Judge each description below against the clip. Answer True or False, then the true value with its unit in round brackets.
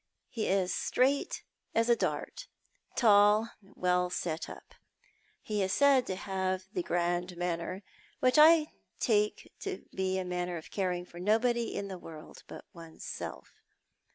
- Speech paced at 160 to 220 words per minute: False (150 wpm)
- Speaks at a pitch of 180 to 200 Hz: True (190 Hz)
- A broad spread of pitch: False (4.2 semitones)